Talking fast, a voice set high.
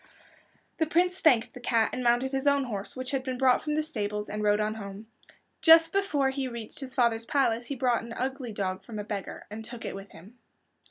Yes: fast, 225 wpm; high, 245 Hz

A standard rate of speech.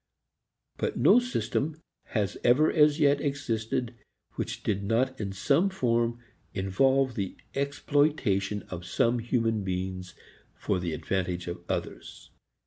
No: slow, 125 wpm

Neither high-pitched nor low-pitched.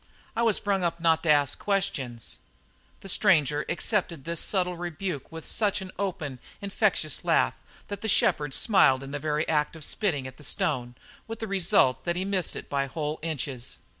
Yes: medium, 165 Hz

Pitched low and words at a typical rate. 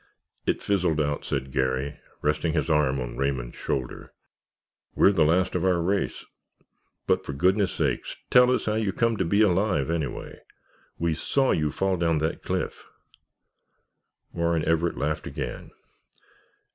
Yes: very low, 85 Hz; average, 145 wpm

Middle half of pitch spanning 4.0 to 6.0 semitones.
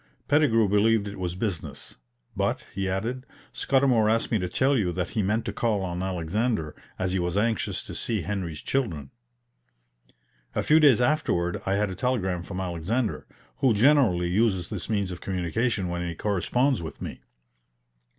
Yes: average, 4.5 semitones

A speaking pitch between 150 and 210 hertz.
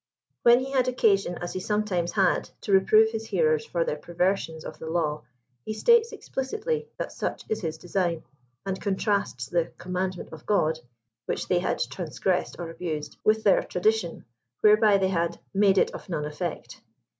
Yes: high, 190 Hz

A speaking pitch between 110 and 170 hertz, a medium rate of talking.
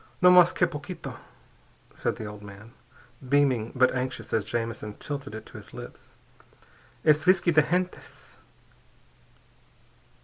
No: low, 135 Hz; slow, 130 wpm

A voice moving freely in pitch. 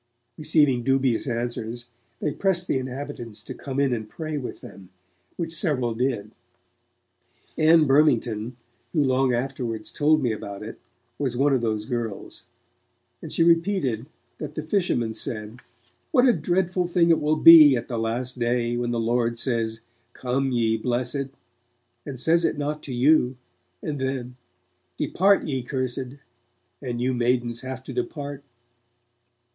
No: average, 4.0 semitones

